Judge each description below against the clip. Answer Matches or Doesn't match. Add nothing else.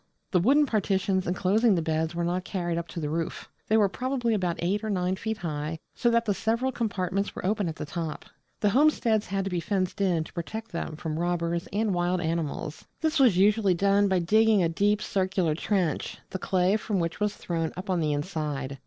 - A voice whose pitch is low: Doesn't match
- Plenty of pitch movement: Doesn't match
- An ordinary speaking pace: Doesn't match